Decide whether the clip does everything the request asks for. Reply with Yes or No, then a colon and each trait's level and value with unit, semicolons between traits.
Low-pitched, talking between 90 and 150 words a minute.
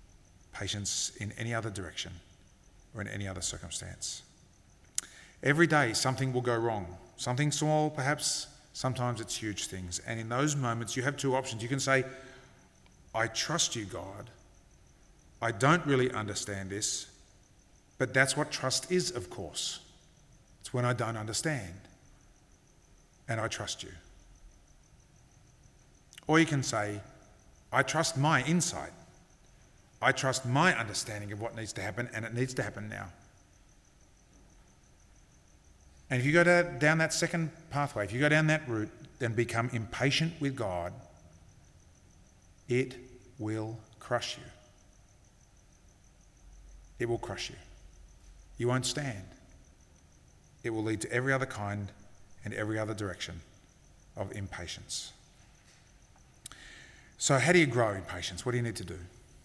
Yes: low, 115 Hz; average, 140 wpm